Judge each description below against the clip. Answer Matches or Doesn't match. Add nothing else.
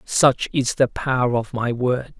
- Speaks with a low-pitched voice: Matches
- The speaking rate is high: Doesn't match